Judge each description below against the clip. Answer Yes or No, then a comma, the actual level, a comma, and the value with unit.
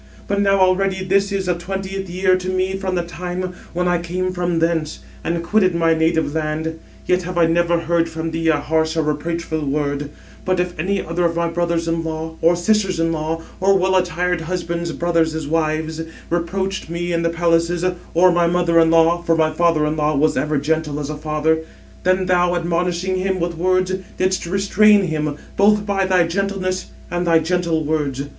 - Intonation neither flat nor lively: No, narrow, 2.3 semitones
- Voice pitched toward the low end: No, medium, 170 Hz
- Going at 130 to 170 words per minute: No, average, 195 wpm